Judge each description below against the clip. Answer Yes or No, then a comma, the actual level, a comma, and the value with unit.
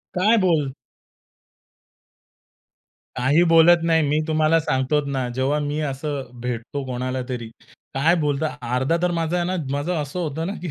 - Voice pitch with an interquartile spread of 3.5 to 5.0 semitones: Yes, average, 3.9 semitones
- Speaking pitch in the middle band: Yes, medium, 150 Hz